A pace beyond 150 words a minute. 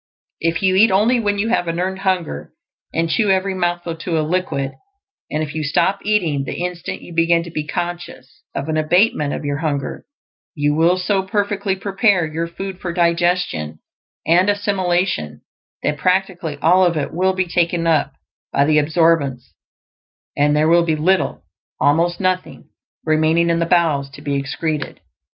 Yes: average, 170 wpm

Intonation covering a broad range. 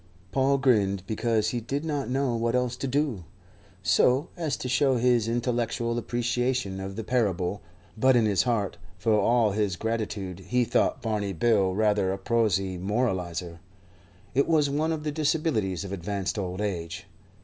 No: average, 4.5 semitones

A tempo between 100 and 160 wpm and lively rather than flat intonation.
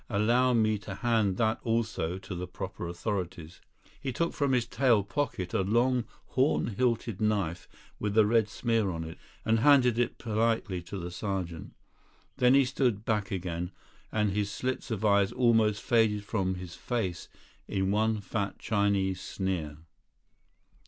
No: average, 155 wpm; average, 3.5 semitones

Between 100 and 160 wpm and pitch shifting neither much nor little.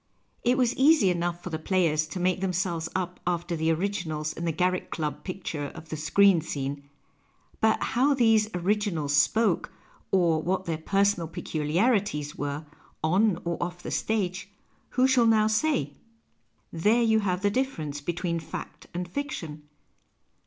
Yes: average, 155 wpm; average, 4.7 semitones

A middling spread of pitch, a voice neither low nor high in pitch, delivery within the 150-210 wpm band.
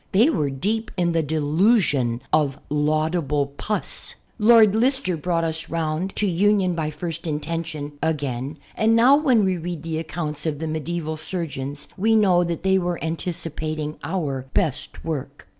Yes: average, 3.8 semitones; medium, 165 Hz; average, 155 wpm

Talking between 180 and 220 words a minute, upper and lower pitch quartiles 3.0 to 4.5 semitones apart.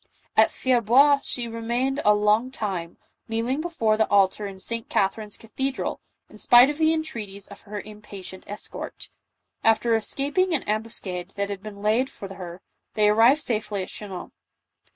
No: average, 160 wpm; average, 3.8 semitones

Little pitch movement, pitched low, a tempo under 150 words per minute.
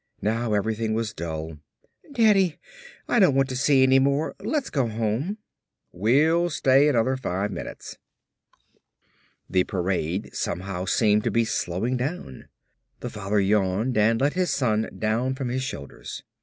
No: average, 5.0 semitones; low, 115 Hz; average, 140 wpm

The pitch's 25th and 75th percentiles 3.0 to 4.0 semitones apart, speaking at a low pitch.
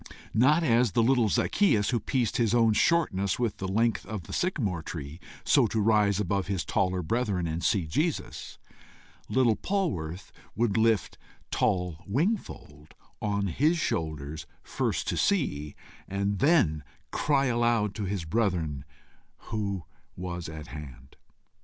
No: wide, 5.5 semitones; low, 100 Hz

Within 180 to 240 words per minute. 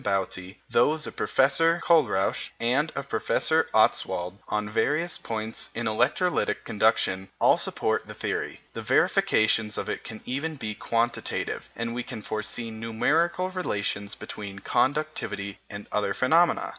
No: slow, 135 wpm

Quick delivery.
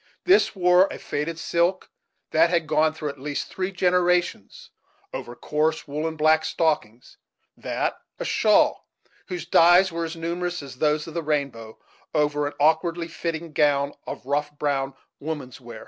No: average, 155 wpm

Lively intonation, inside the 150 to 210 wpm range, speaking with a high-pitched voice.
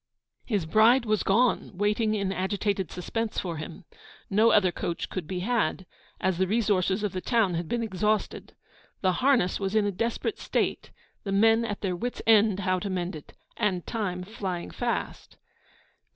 No: average, 3.1 semitones; average, 170 wpm; high, 200 Hz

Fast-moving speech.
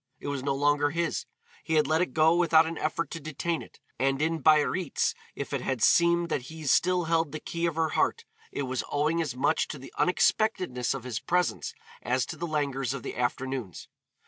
Yes: fast, 210 wpm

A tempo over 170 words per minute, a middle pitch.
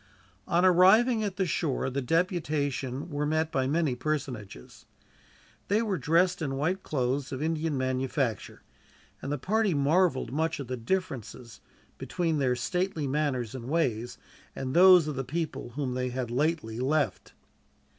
No: average, 150 wpm; medium, 145 Hz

